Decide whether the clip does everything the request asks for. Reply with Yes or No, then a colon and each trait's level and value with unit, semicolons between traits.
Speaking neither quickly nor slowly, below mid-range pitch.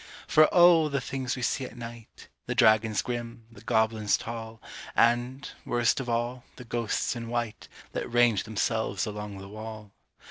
Yes: average, 165 wpm; low, 115 Hz